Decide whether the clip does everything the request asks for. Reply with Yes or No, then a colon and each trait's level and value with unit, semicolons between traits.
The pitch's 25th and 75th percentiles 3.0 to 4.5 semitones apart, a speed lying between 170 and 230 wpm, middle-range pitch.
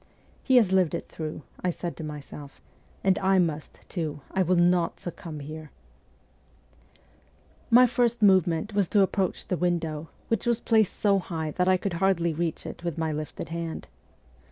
Yes: average, 3.4 semitones; average, 180 wpm; medium, 175 Hz